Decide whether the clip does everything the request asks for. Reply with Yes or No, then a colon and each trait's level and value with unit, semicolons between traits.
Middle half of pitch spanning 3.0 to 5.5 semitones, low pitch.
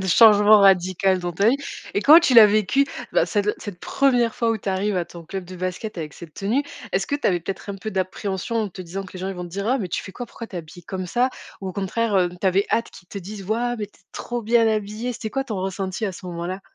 No: average, 3.3 semitones; high, 200 Hz